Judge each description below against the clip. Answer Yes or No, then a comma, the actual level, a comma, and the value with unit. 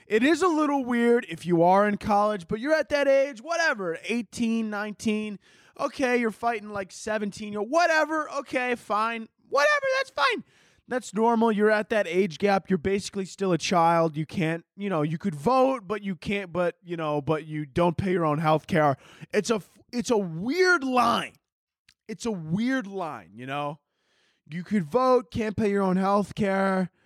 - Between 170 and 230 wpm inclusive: Yes, average, 185 wpm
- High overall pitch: Yes, high, 210 Hz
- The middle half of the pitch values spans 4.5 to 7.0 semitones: Yes, average, 5.2 semitones